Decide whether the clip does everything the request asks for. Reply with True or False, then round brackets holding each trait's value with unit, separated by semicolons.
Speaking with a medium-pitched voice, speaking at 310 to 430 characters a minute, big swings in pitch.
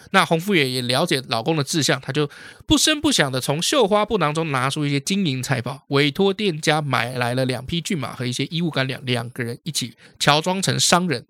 False (145 Hz; 325 characters per minute; 4.8 semitones)